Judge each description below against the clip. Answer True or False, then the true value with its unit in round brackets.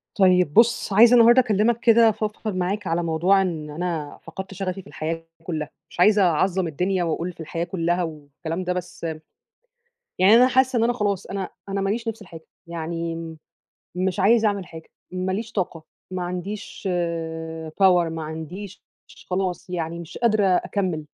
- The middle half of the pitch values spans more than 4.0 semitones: False (3.5 semitones)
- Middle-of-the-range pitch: True (180 Hz)